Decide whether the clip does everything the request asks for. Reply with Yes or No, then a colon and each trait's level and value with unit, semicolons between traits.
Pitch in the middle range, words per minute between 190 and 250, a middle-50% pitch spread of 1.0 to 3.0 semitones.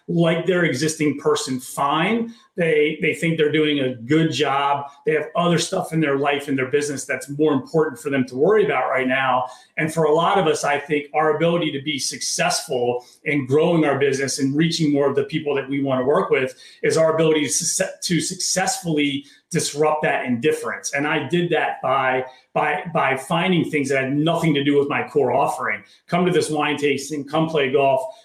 Yes: medium, 150 Hz; fast, 205 wpm; narrow, 2.5 semitones